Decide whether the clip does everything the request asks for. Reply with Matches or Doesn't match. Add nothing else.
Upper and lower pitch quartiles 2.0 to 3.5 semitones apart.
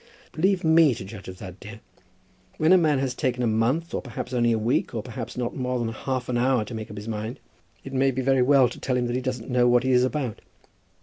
Matches